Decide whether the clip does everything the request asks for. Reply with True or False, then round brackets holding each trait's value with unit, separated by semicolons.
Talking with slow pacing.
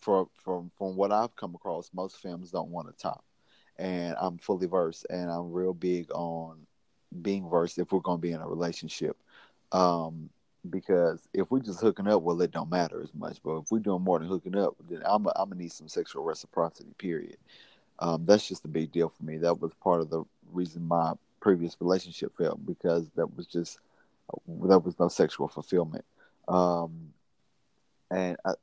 False (195 wpm)